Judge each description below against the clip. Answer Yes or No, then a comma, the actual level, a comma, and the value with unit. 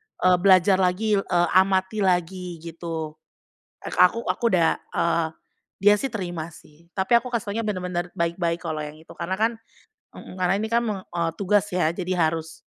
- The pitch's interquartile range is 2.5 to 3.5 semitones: Yes, average, 3.2 semitones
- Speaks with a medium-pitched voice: Yes, medium, 180 Hz